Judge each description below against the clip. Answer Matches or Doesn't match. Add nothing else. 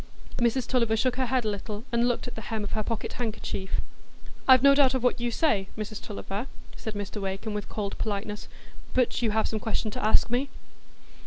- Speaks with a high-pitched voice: Matches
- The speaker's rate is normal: Doesn't match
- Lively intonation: Doesn't match